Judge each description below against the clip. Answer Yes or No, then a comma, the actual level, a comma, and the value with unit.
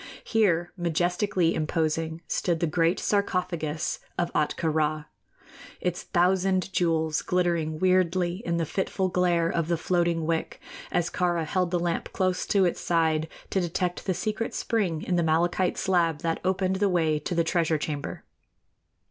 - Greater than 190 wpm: No, average, 155 wpm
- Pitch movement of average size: No, narrow, 2.1 semitones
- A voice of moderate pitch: Yes, medium, 175 Hz